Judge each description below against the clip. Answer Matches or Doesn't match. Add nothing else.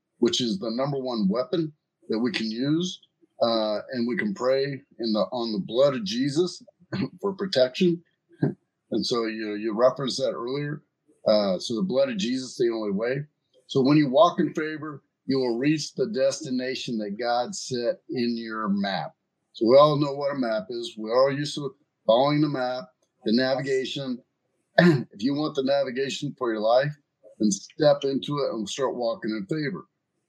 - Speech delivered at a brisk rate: Doesn't match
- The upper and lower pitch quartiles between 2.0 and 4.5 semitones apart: Doesn't match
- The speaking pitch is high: Doesn't match